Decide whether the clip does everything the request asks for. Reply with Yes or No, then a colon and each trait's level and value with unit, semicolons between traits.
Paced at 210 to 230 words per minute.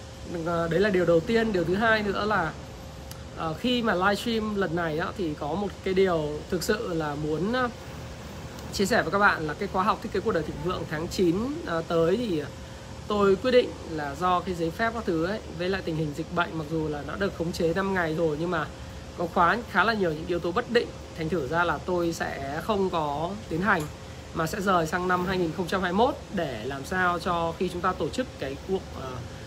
Yes: average, 225 wpm